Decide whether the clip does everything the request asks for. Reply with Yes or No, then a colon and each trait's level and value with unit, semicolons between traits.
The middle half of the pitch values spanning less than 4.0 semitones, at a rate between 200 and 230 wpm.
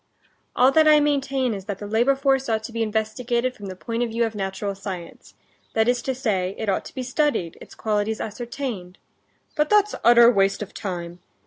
No: average, 4.5 semitones; fast, 205 wpm